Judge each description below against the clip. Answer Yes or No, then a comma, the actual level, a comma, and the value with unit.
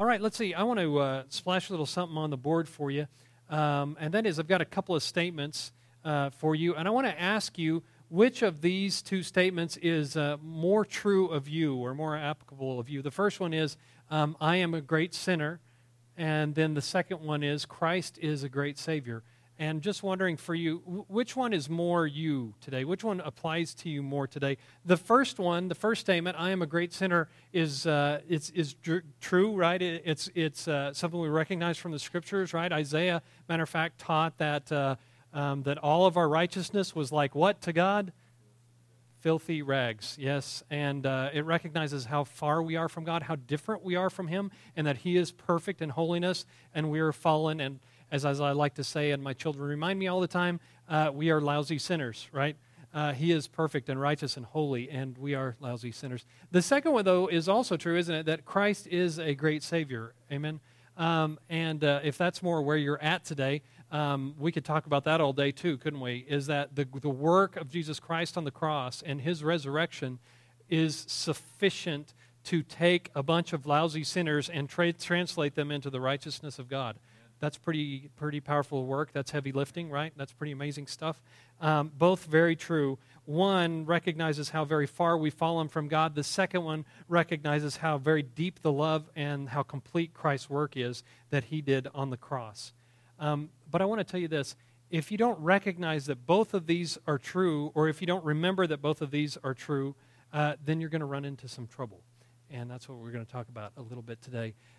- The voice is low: No, medium, 155 Hz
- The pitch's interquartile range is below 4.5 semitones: Yes, average, 3.4 semitones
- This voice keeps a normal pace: No, fast, 210 wpm